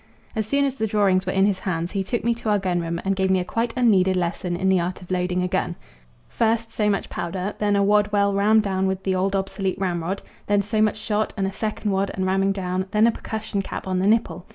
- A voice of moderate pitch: No, high, 195 Hz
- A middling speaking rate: No, fast, 260 wpm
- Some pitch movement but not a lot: No, narrow, 2.1 semitones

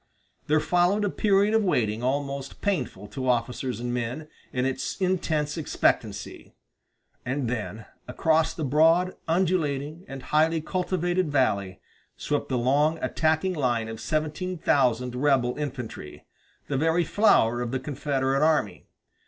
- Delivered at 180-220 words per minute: No, slow, 135 wpm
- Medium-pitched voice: Yes, medium, 145 Hz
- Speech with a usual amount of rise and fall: Yes, average, 4.5 semitones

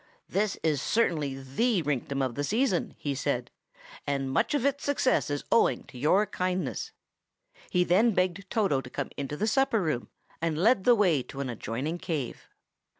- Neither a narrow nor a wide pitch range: No, wide, 7.3 semitones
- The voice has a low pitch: No, medium, 165 Hz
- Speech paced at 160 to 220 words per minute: Yes, average, 175 wpm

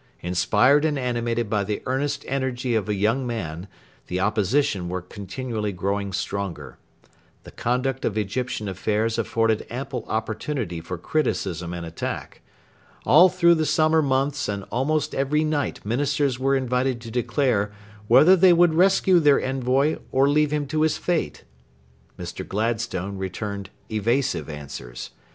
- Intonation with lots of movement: Yes, wide, 5.8 semitones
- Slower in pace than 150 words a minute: Yes, average, 140 wpm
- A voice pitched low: Yes, low, 120 Hz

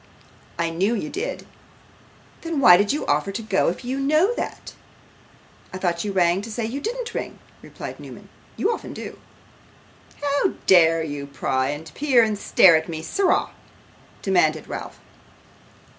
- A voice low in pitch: No, high, 195 Hz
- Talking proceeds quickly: No, average, 160 wpm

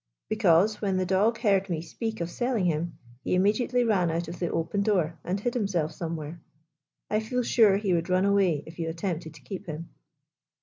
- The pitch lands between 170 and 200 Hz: Yes, medium, 185 Hz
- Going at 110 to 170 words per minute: No, fast, 205 wpm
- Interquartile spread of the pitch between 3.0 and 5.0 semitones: Yes, average, 4.1 semitones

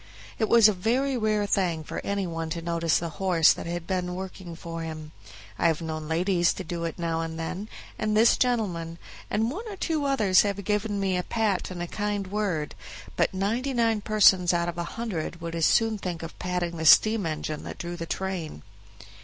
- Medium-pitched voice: Yes, medium, 180 Hz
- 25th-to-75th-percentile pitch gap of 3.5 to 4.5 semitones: Yes, average, 4.1 semitones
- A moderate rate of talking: No, fast, 210 wpm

